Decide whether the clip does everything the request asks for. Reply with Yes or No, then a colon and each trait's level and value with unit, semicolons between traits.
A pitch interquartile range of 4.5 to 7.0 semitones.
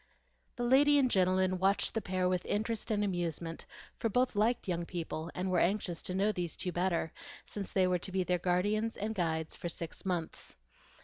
No: average, 3.1 semitones